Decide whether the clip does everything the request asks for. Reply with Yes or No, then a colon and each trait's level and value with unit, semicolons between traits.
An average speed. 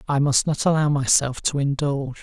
Yes: average, 190 wpm